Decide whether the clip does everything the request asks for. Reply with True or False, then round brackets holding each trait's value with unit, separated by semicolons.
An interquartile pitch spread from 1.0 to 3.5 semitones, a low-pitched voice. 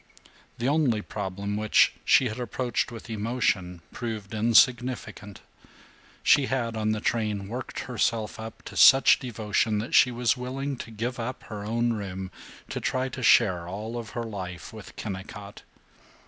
True (2.9 semitones; 110 Hz)